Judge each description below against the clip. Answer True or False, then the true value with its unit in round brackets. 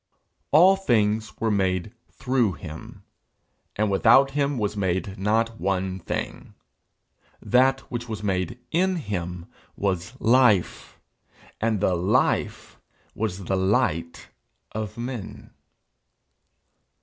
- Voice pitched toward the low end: True (105 Hz)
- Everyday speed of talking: False (105 wpm)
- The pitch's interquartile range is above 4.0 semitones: True (4.5 semitones)